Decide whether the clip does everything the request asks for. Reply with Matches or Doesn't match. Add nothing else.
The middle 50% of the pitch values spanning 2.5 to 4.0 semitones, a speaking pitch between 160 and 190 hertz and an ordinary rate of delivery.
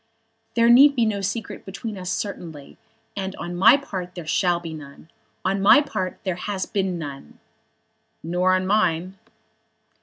Matches